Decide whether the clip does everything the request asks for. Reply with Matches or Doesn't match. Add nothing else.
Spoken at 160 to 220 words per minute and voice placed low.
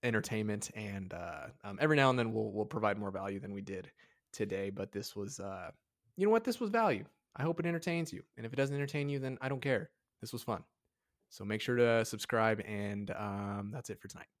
Doesn't match